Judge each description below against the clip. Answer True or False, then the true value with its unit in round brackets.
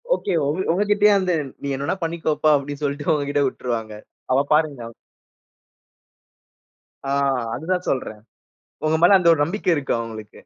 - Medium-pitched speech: True (150 Hz)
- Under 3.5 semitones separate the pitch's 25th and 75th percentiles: False (4.3 semitones)